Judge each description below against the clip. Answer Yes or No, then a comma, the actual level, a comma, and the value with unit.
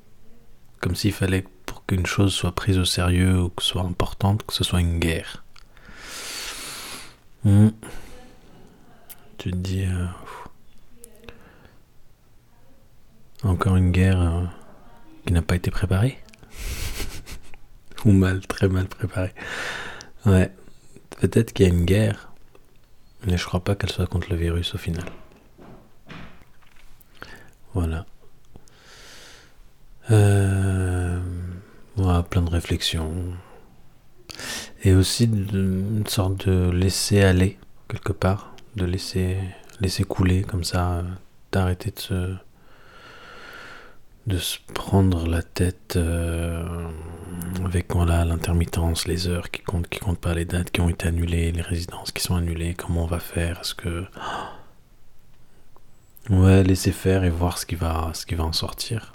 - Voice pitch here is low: Yes, very low, 95 Hz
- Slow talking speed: Yes, slow, 130 wpm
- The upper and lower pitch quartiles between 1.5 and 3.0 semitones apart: Yes, narrow, 2.5 semitones